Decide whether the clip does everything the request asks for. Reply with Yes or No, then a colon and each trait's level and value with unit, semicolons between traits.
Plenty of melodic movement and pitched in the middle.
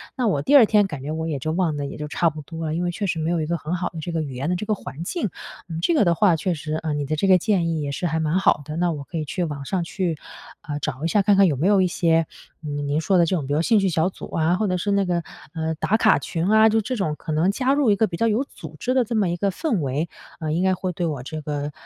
No: average, 4.0 semitones; medium, 170 Hz